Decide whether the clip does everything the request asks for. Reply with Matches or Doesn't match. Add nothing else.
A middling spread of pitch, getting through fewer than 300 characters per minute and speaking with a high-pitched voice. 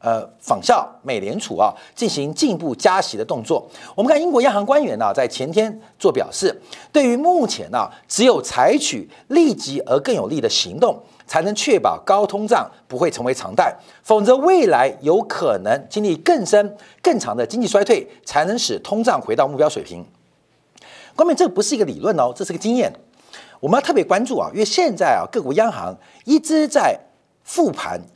Doesn't match